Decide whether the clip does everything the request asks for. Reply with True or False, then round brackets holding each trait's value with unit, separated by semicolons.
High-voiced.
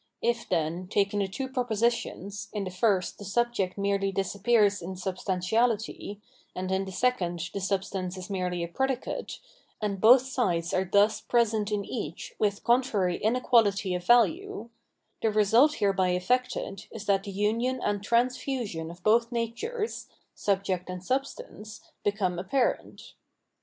True (205 Hz)